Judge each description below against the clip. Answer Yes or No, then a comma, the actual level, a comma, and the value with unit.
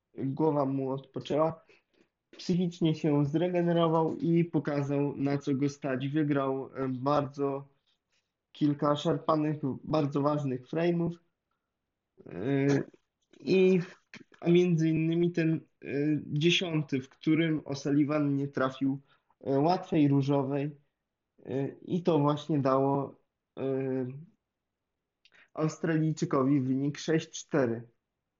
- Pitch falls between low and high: Yes, medium, 145 Hz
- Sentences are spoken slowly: Yes, slow, 80 wpm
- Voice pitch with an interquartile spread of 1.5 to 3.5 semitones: Yes, average, 2.8 semitones